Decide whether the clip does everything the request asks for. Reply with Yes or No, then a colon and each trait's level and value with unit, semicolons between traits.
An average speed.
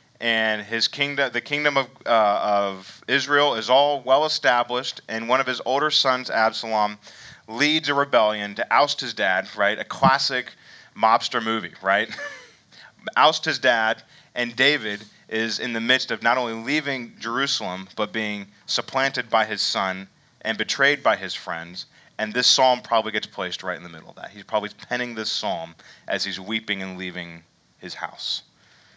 Yes: average, 170 wpm